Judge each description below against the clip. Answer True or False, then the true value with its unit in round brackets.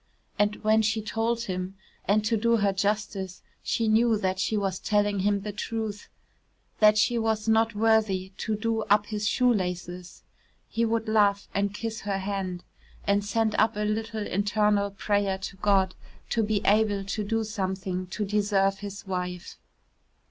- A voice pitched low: False (205 Hz)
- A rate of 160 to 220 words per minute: True (165 wpm)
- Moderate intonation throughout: False (2.1 semitones)